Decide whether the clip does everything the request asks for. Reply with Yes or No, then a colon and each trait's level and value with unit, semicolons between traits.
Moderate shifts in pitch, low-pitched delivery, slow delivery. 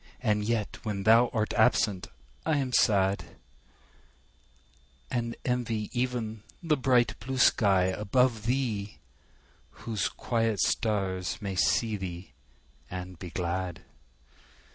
Yes: average, 3.8 semitones; low, 110 Hz; slow, 110 wpm